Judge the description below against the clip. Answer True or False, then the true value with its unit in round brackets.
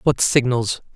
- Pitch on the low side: True (125 Hz)